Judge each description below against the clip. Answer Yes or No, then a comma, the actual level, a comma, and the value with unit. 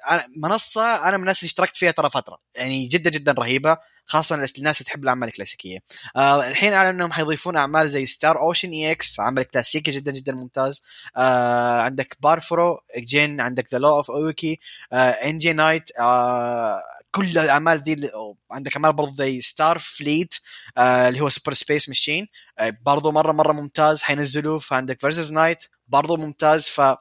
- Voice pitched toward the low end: No, medium, 150 Hz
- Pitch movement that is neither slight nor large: Yes, average, 3.5 semitones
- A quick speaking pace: Yes, fast, 160 wpm